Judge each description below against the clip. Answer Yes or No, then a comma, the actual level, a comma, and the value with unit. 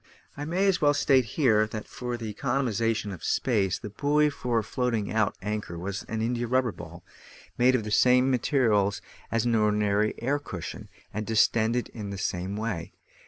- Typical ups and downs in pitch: Yes, average, 3.4 semitones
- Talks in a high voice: No, low, 115 Hz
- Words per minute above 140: Yes, average, 175 wpm